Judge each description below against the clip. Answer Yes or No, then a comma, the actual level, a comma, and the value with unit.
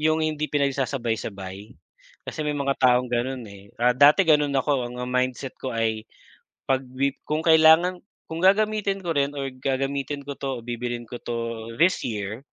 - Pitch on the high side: No, low, 135 Hz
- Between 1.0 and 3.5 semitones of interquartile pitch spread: No, average, 4.0 semitones